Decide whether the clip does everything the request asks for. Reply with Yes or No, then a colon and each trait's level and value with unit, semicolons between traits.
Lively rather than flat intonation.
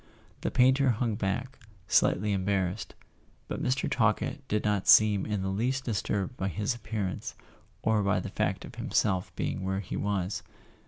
No: average, 3.5 semitones